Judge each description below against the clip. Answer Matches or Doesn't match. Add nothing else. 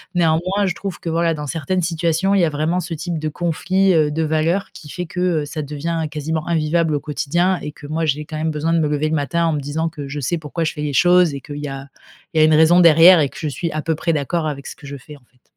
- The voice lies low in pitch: Doesn't match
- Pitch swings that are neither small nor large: Doesn't match